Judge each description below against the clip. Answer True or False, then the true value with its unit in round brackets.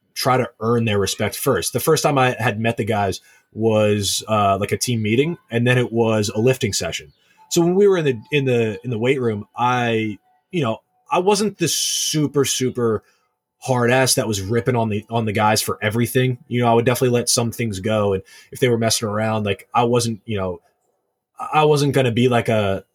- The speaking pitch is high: False (120 Hz)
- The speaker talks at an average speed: False (225 wpm)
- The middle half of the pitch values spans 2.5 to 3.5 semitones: True (3.1 semitones)